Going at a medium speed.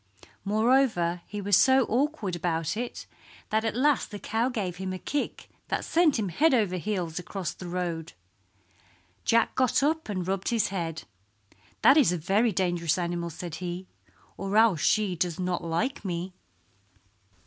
Yes: average, 160 wpm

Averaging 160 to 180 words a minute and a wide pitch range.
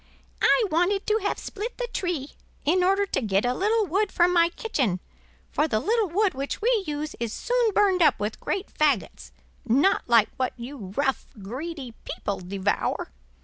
Yes: average, 175 wpm; wide, 8.8 semitones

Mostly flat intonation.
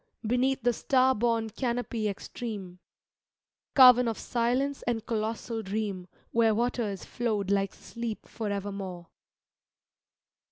No: average, 3.1 semitones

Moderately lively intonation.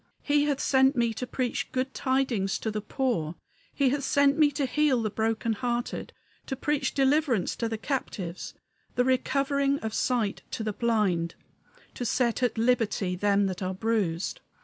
Yes: average, 4.1 semitones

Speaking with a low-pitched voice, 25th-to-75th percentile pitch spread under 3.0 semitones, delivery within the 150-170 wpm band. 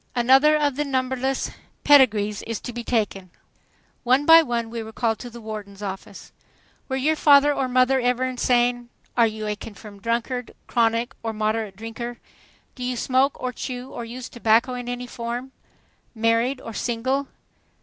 No: high, 240 Hz; narrow, 2.4 semitones; average, 165 wpm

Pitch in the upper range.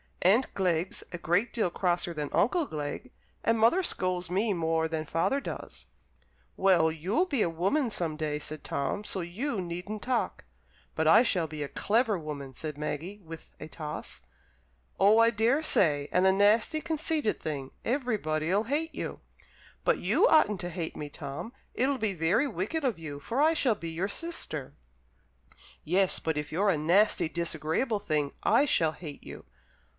No: medium, 180 Hz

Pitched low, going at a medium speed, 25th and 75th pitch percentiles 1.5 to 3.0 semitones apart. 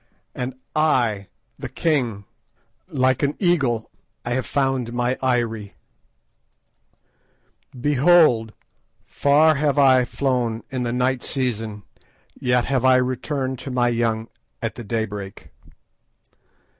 No: low, 125 Hz; slow, 105 wpm; average, 2.7 semitones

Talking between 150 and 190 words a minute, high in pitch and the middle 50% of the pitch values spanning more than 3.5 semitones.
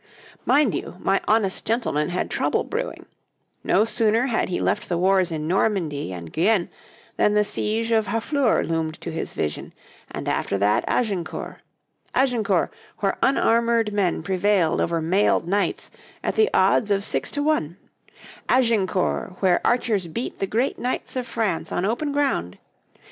Yes: average, 155 wpm; high, 205 Hz; average, 4.8 semitones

